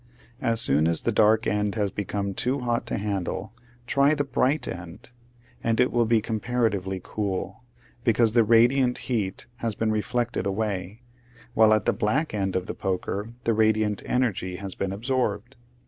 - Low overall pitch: Yes, low, 110 Hz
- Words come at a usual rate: Yes, average, 165 wpm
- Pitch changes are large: No, average, 3.2 semitones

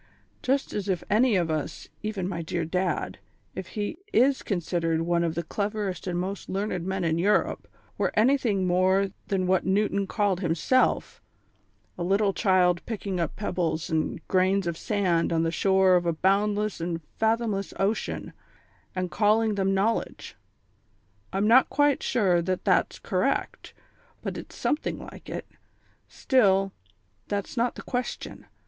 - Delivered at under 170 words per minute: Yes, average, 150 wpm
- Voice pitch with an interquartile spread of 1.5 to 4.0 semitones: Yes, average, 3.1 semitones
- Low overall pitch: No, high, 195 Hz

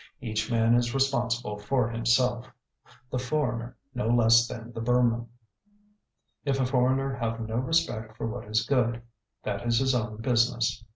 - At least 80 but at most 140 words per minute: No, average, 155 wpm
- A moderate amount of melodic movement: No, narrow, 1.7 semitones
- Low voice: Yes, low, 120 Hz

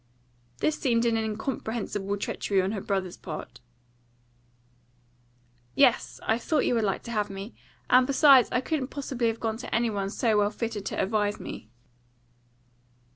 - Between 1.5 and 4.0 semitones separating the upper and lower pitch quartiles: Yes, average, 3.3 semitones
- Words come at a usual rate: Yes, average, 155 wpm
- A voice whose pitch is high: Yes, high, 225 Hz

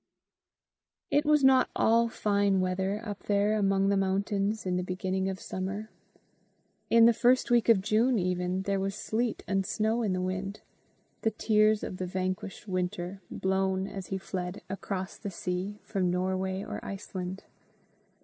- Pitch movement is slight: Yes, narrow, 2.3 semitones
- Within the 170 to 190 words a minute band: No, average, 160 wpm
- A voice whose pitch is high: Yes, high, 195 Hz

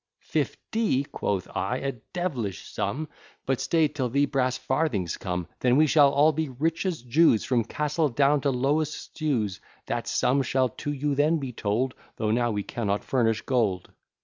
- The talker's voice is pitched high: No, low, 135 Hz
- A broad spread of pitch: No, average, 4.2 semitones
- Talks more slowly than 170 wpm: No, average, 175 wpm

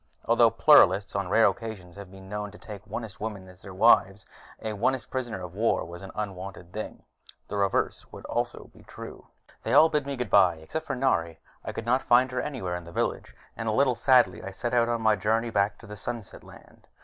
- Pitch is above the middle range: No, low, 105 Hz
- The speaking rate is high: Yes, fast, 220 wpm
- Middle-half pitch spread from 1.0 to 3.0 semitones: No, average, 3.8 semitones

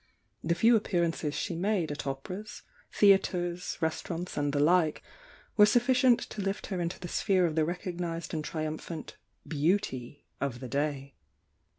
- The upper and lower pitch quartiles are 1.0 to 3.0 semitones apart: No, average, 4.1 semitones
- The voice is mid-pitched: Yes, medium, 170 Hz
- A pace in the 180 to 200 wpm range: No, average, 155 wpm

